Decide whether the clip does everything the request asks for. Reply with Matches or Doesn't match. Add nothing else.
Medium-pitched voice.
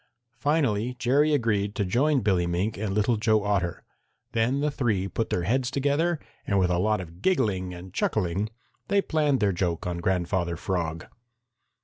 Doesn't match